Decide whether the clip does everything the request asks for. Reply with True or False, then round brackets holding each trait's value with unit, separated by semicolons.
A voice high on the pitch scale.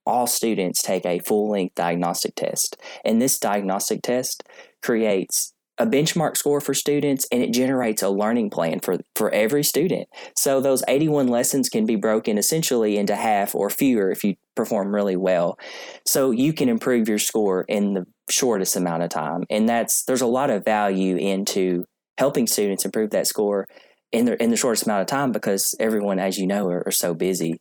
False (105 Hz)